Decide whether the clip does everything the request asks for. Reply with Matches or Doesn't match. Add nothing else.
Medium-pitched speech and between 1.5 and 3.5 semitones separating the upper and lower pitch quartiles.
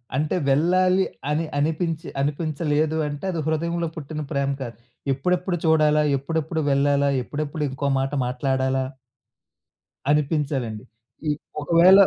Matches